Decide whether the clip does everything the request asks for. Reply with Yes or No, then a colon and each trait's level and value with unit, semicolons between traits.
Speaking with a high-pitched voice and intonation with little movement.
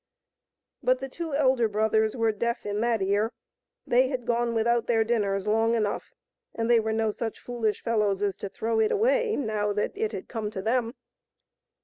Yes: high, 225 Hz; narrow, 2.2 semitones